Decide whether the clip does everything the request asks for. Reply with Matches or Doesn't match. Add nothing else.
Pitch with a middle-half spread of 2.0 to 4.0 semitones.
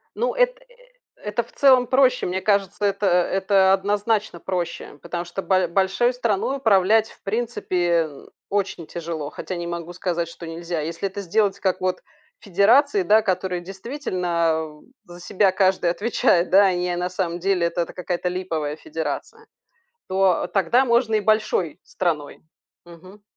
Matches